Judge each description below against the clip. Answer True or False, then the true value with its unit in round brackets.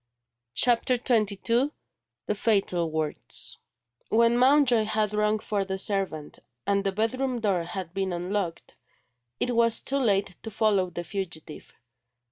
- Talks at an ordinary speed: False (130 wpm)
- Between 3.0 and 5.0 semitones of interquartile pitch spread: True (3.6 semitones)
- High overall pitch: True (210 Hz)